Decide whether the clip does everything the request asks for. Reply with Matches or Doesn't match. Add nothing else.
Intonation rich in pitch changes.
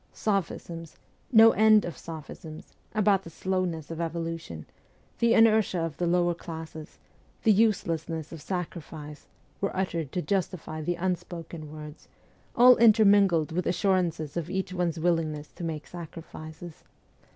Doesn't match